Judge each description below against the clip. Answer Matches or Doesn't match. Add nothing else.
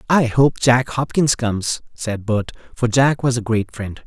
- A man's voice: Matches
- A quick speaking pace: Doesn't match